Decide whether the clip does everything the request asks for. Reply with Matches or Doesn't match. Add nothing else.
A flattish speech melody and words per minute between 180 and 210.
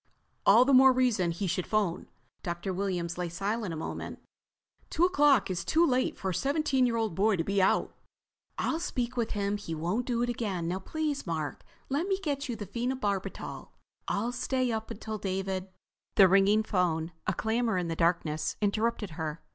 Doesn't match